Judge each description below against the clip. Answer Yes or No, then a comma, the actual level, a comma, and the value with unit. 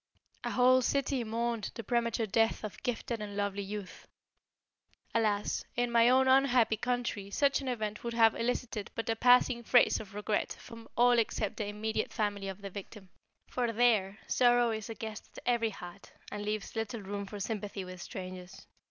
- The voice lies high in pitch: Yes, high, 220 Hz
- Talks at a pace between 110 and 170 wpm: No, average, 180 wpm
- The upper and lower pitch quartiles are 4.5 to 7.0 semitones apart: No, average, 2.8 semitones